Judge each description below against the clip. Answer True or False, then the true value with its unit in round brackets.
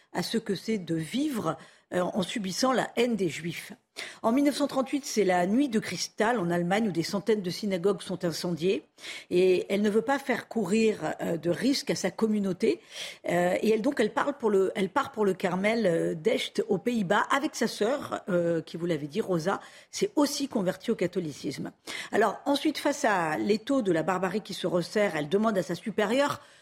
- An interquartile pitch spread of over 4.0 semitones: True (4.7 semitones)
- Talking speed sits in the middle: True (190 wpm)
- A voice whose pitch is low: False (205 Hz)